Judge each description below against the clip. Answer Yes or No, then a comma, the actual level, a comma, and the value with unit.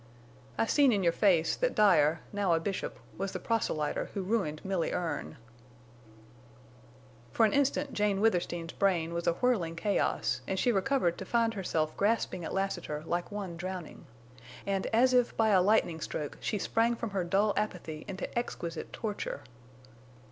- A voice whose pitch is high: Yes, high, 195 Hz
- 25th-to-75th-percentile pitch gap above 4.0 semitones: Yes, average, 4.6 semitones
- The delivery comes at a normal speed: Yes, average, 160 wpm